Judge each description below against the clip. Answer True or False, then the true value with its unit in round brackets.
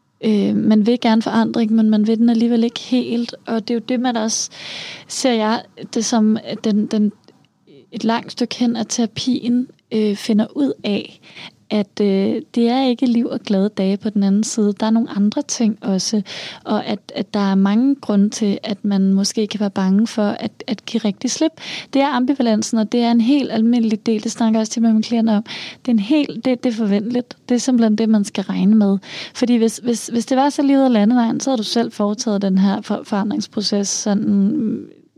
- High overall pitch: True (225 Hz)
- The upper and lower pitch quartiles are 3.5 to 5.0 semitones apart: False (2.5 semitones)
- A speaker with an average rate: True (215 wpm)